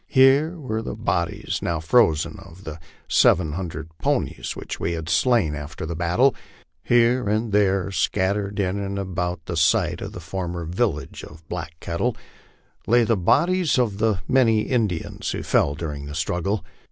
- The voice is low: Yes, very low, 95 Hz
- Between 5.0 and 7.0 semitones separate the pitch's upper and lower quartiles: Yes, average, 5.3 semitones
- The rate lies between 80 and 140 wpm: No, average, 165 wpm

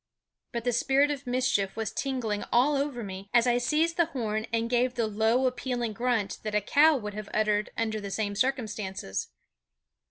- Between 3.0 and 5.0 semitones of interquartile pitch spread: Yes, average, 3.4 semitones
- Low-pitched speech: No, high, 235 Hz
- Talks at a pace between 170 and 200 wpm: Yes, average, 185 wpm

